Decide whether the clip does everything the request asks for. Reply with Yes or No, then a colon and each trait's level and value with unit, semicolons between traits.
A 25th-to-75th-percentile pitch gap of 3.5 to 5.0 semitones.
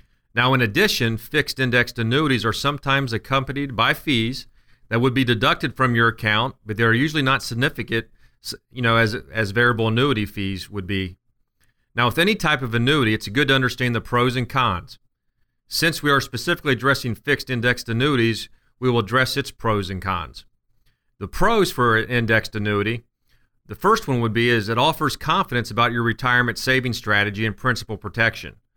No: average, 3.0 semitones